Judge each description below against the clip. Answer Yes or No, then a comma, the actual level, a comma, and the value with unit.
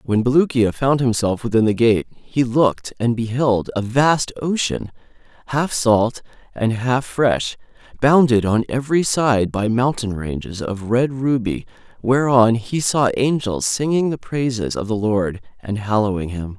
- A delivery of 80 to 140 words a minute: No, average, 150 wpm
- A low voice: Yes, low, 120 Hz